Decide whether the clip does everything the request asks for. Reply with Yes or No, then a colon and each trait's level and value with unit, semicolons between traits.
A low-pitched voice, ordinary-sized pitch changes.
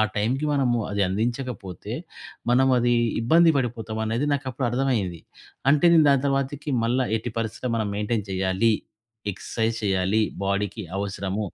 Yes: low, 115 Hz; average, 4.3 semitones